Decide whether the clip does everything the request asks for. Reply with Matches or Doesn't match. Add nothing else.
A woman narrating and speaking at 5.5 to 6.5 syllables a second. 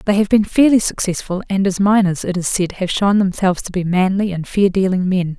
Matches